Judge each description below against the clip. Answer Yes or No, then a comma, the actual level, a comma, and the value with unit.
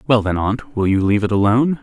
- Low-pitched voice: Yes, low, 110 Hz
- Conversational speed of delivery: No, fast, 265 wpm